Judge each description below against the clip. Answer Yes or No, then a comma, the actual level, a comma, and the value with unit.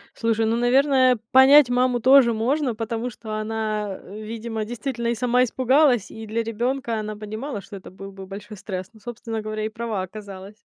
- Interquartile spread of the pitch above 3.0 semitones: No, narrow, 2.6 semitones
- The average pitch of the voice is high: Yes, high, 225 Hz